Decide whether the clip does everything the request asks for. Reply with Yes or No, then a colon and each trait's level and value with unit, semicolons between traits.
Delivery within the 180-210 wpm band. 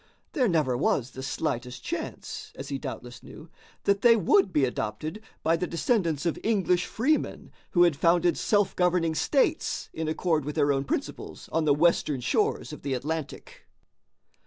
No: average, 165 wpm